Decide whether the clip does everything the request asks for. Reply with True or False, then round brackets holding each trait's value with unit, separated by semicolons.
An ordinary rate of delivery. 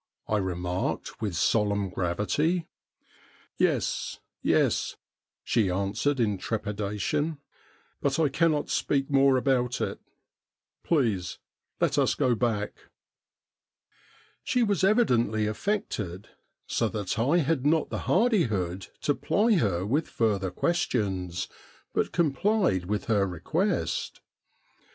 False (110 wpm)